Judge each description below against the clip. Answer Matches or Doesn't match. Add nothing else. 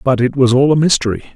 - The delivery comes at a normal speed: Doesn't match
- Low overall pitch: Matches